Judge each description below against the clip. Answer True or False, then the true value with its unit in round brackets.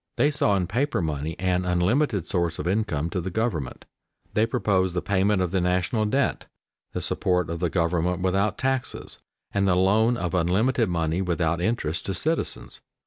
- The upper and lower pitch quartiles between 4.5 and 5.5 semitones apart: False (3.7 semitones)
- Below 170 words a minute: False (175 wpm)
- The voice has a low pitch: True (95 Hz)